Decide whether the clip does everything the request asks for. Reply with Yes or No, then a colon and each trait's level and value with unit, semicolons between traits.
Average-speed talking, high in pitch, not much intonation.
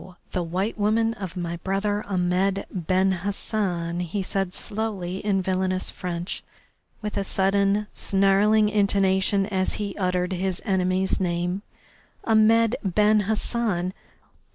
No: slow, 120 wpm; high, 195 Hz; narrow, 2.2 semitones